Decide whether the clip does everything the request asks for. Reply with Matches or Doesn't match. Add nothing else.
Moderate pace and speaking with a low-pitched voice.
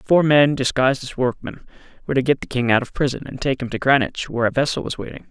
Doesn't match